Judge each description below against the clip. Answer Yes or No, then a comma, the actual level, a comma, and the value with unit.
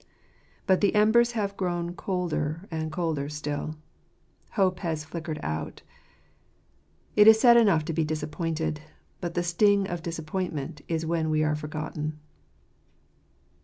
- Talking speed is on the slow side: Yes, slow, 130 wpm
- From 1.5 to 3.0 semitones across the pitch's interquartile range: No, average, 3.5 semitones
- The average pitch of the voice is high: No, medium, 165 Hz